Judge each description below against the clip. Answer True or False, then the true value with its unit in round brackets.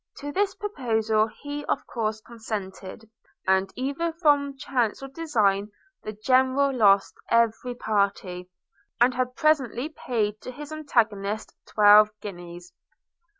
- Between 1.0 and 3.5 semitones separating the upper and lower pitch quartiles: False (5.1 semitones)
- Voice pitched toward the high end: True (230 Hz)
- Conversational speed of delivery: False (120 wpm)